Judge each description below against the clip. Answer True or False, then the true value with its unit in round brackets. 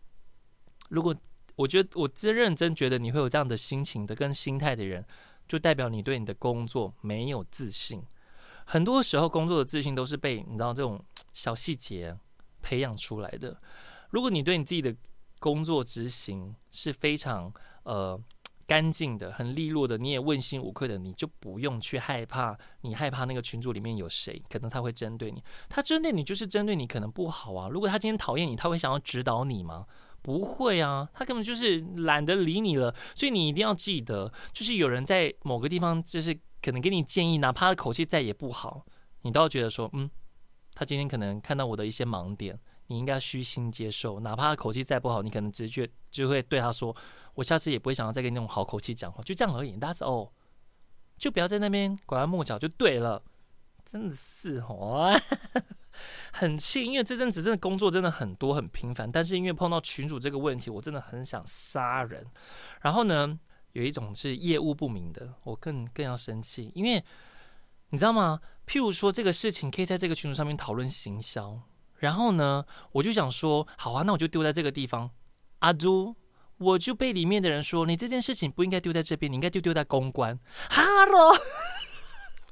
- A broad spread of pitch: True (6.2 semitones)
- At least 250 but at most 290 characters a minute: False (305 characters per minute)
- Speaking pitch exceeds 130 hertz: True (140 Hz)